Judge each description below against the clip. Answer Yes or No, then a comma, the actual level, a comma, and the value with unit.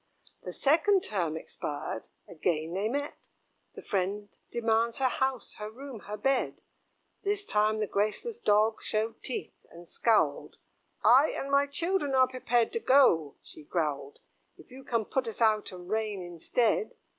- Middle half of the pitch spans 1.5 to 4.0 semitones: No, average, 5.2 semitones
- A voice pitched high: Yes, high, 225 Hz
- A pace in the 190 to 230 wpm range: No, average, 155 wpm